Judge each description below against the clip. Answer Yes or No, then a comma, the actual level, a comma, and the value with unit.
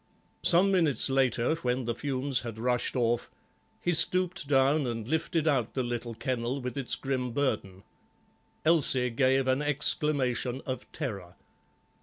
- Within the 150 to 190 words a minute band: No, average, 140 wpm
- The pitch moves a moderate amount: Yes, average, 3.2 semitones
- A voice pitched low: Yes, low, 130 Hz